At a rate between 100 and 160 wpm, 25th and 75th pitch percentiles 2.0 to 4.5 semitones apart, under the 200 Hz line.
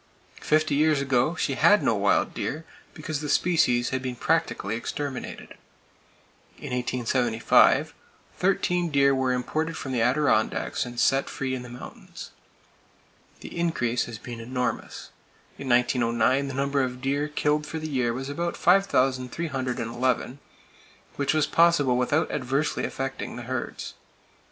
Yes: slow, 135 wpm; average, 3.6 semitones; low, 135 Hz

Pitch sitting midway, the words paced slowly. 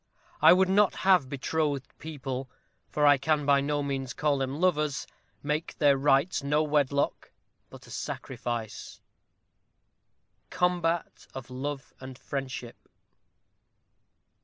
Yes: medium, 145 Hz; slow, 115 wpm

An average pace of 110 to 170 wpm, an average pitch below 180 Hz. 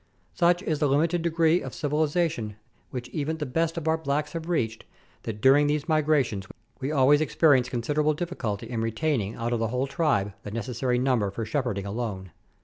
No: average, 185 wpm; medium, 140 Hz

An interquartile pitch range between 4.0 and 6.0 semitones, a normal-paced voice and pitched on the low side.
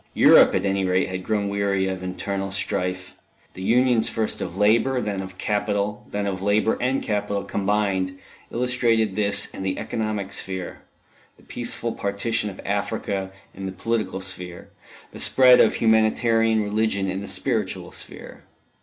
No: narrow, 2.6 semitones; average, 155 wpm; low, 100 Hz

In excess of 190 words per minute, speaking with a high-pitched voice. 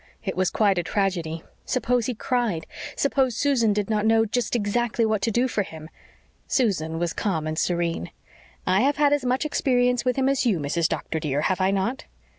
Yes: average, 200 wpm; high, 215 Hz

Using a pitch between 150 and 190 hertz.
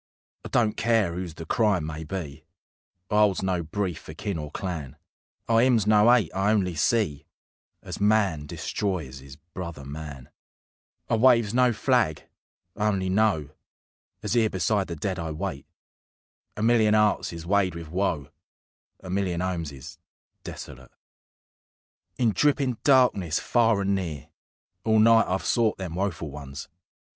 No: very low, 95 Hz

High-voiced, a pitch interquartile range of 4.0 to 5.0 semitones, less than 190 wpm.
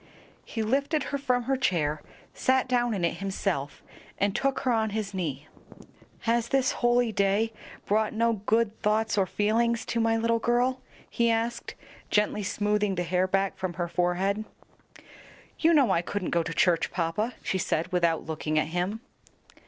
Yes: high, 210 Hz; average, 4.4 semitones; average, 170 wpm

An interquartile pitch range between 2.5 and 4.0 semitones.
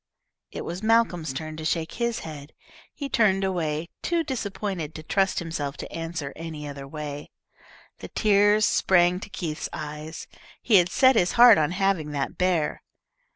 No: average, 4.7 semitones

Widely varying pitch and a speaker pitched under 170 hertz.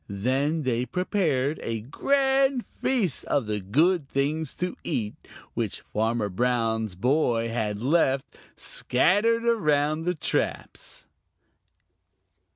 Yes: wide, 7.5 semitones; medium, 140 Hz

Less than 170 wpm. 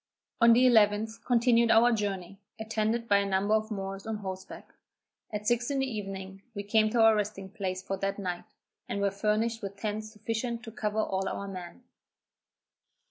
No: average, 180 wpm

